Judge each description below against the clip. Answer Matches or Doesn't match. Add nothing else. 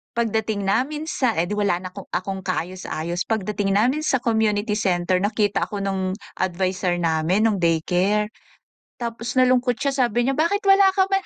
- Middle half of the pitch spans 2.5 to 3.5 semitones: Doesn't match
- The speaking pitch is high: Matches